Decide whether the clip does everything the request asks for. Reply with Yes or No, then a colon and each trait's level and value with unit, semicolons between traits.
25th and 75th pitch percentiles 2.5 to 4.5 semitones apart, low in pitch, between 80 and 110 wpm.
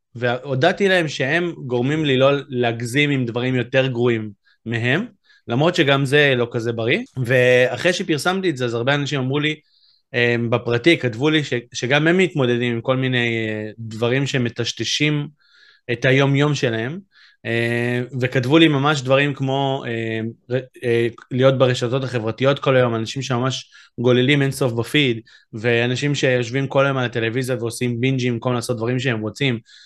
No: average, 2.9 semitones; low, 130 Hz; average, 140 wpm